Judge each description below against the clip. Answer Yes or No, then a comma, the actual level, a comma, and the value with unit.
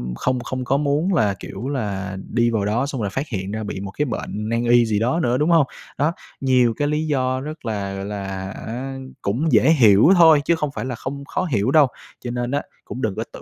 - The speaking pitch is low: Yes, low, 125 Hz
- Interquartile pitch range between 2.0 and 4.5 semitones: No, average, 5.3 semitones